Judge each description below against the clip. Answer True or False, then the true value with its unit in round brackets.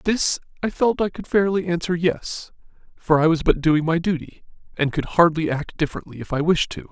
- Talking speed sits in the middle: False (215 wpm)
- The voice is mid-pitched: True (170 Hz)